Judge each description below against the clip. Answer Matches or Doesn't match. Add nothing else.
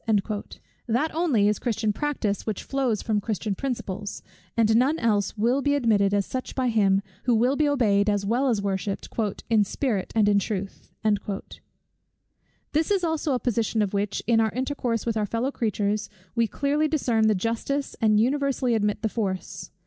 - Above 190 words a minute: Doesn't match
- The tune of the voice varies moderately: Matches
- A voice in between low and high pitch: Doesn't match